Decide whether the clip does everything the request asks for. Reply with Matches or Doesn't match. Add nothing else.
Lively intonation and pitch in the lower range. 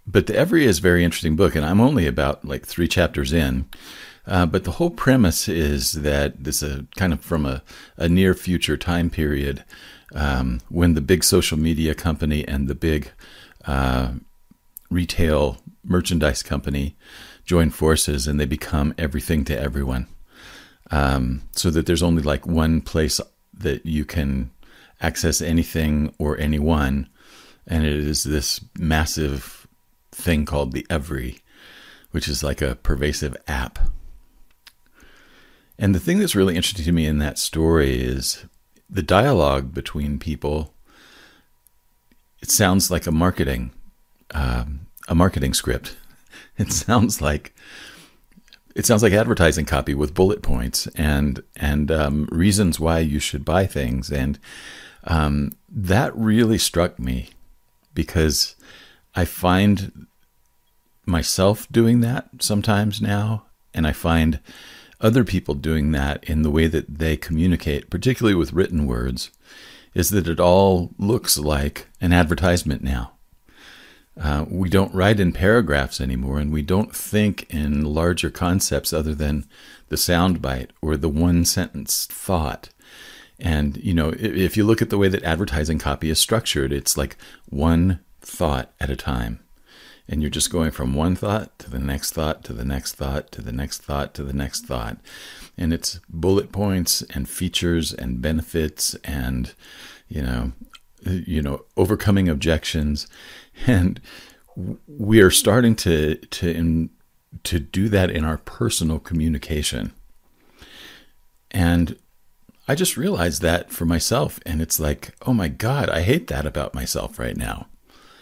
Doesn't match